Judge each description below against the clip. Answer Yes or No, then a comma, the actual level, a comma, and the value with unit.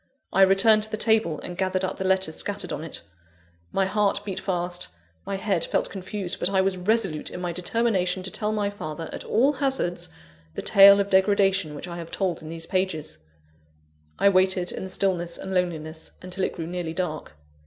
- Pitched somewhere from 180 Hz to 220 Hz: Yes, medium, 185 Hz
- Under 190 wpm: No, average, 195 wpm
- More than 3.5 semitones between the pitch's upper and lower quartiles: No, narrow, 2.4 semitones